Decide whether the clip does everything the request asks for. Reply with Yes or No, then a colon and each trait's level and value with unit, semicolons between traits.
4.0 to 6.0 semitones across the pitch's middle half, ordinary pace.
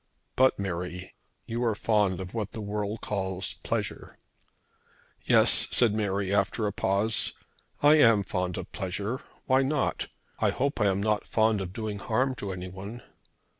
No: average, 2.9 semitones; average, 155 wpm